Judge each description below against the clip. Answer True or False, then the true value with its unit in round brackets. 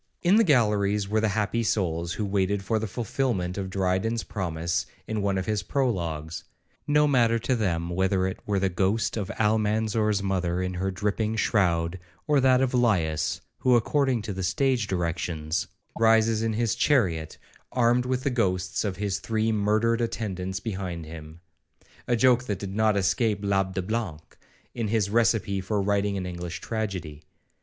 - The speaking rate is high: False (170 wpm)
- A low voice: True (100 Hz)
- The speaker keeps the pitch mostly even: False (3.6 semitones)